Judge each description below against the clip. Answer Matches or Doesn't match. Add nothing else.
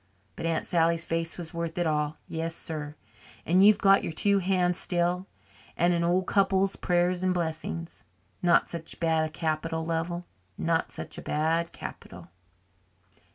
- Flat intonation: Matches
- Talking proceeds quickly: Doesn't match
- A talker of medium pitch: Matches